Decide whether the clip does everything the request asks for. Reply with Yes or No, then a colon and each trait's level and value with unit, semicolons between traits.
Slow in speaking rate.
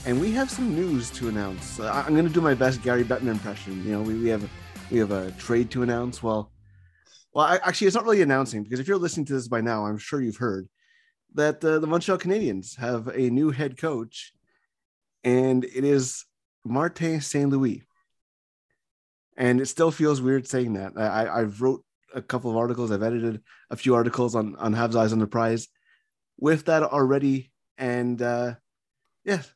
No: average, 195 wpm